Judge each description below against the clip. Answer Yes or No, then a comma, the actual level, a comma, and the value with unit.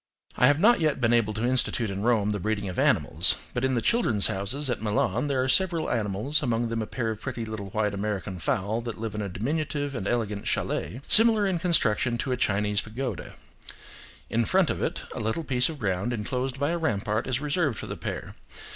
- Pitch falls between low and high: No, low, 120 Hz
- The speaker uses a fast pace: Yes, fast, 220 wpm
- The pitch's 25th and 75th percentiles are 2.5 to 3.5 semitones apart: No, average, 4.8 semitones